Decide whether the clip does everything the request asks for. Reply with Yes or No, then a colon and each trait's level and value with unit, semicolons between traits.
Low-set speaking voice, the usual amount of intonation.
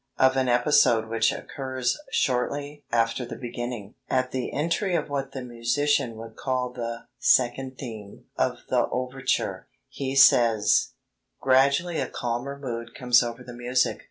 No: low, 125 Hz; narrow, 2.3 semitones